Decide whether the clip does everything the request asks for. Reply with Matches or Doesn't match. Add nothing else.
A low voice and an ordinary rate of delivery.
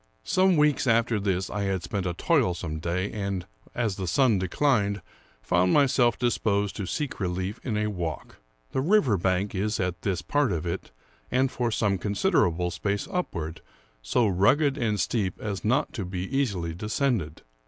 Matches